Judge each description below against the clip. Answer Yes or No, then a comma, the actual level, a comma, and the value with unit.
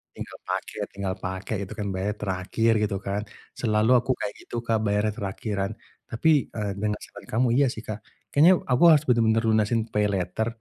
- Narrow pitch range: Yes, narrow, 2.2 semitones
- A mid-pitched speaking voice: No, low, 105 Hz